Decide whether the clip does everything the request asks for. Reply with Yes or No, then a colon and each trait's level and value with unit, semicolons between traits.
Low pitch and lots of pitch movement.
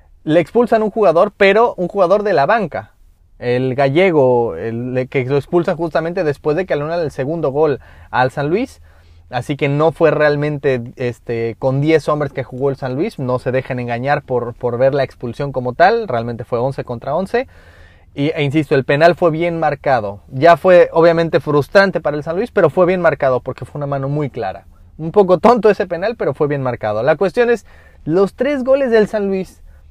No: medium, 145 Hz; wide, 6.0 semitones